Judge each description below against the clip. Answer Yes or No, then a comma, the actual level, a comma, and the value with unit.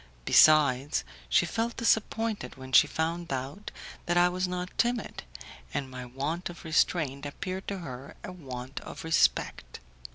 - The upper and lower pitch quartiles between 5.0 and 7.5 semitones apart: Yes, wide, 5.5 semitones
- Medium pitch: Yes, medium, 160 Hz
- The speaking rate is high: No, average, 150 wpm